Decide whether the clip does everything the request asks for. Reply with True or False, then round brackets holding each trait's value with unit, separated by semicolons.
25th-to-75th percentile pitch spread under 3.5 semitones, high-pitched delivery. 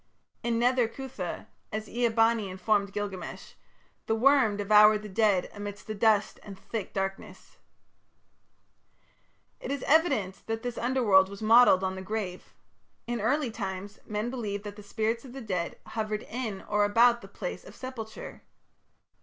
True (2.8 semitones; 215 Hz)